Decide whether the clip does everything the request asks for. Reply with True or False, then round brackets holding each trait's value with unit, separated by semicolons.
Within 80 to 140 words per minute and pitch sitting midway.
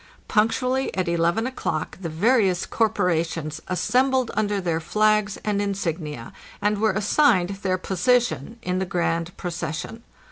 False (135 wpm; 195 Hz)